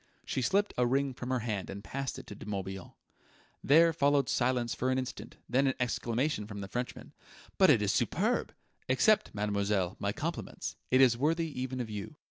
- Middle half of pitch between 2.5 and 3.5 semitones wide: No, average, 4.6 semitones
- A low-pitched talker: Yes, low, 125 Hz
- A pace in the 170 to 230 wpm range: Yes, average, 190 wpm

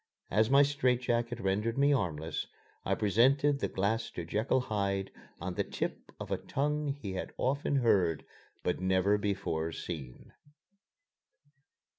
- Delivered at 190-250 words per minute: No, average, 140 wpm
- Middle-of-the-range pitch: No, low, 105 Hz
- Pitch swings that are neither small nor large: No, wide, 6.0 semitones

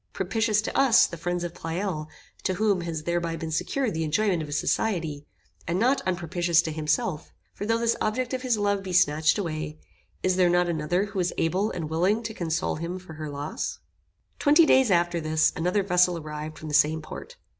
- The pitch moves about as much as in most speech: Yes, average, 4.3 semitones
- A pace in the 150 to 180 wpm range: No, average, 200 wpm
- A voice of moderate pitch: Yes, medium, 175 Hz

